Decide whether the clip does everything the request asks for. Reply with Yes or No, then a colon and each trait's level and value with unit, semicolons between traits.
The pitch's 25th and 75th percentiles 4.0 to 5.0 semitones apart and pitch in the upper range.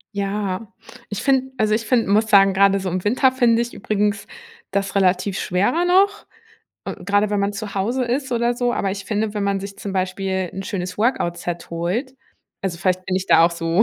No: average, 3.5 semitones; high, 200 Hz